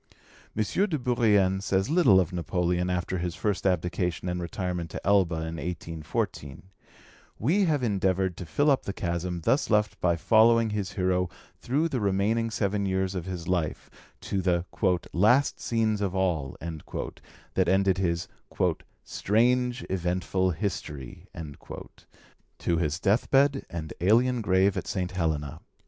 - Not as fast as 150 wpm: Yes, average, 140 wpm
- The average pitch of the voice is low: Yes, very low, 95 Hz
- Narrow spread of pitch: No, average, 3.7 semitones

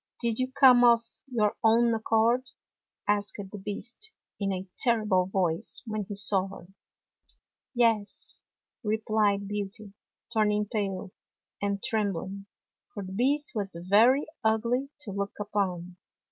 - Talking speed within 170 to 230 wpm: No, slow, 135 wpm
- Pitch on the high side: Yes, high, 210 Hz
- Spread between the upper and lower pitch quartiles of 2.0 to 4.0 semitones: Yes, average, 2.9 semitones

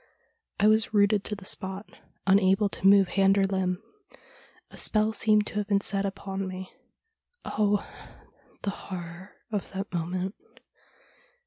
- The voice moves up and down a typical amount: No, narrow, 1.6 semitones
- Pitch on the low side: No, high, 195 Hz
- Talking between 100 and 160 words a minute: Yes, average, 140 wpm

